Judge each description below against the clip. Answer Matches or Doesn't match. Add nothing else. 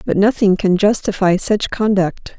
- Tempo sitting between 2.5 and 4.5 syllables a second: Matches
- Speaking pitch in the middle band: Doesn't match